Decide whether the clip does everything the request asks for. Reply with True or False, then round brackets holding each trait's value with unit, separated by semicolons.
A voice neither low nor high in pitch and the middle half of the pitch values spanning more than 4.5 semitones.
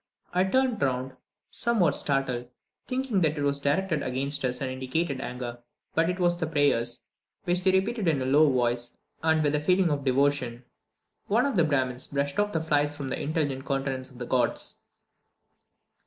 True (145 Hz; 5.0 semitones)